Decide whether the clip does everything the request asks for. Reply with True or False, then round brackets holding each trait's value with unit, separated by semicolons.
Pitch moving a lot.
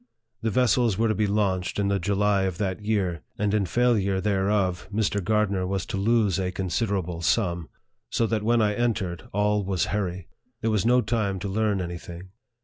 False (2.5 semitones)